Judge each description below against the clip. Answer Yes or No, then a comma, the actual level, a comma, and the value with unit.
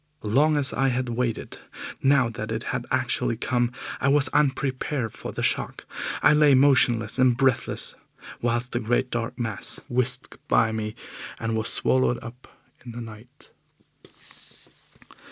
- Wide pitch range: No, narrow, 2.6 semitones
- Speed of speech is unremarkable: Yes, average, 145 wpm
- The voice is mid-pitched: No, low, 125 Hz